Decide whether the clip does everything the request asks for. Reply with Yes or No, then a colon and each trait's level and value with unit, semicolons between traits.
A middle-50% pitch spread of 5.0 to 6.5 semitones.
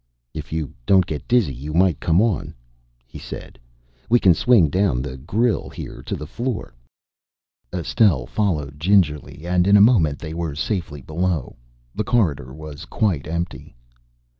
Yes: average, 5.3 semitones